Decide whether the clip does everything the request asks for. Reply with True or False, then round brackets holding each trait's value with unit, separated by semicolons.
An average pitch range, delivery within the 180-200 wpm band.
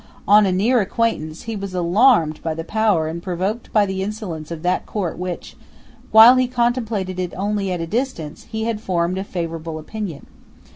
True (4.4 semitones; 190 wpm)